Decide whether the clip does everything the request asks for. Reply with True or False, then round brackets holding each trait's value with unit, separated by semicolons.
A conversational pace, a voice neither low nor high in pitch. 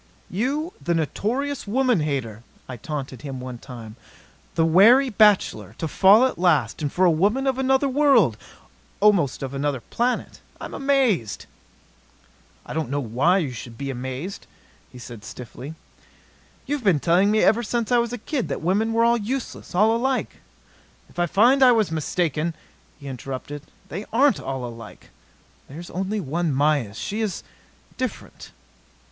True (160 wpm; 175 Hz)